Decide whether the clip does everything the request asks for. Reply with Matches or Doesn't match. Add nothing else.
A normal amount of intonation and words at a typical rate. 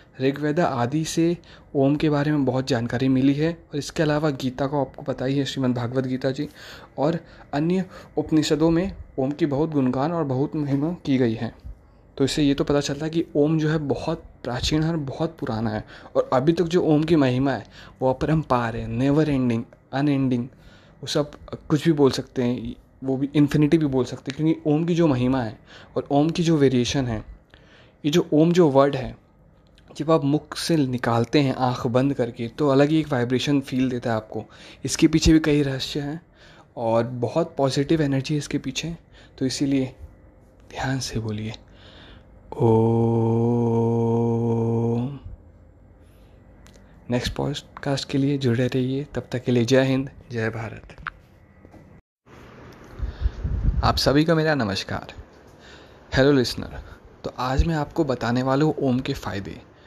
Matches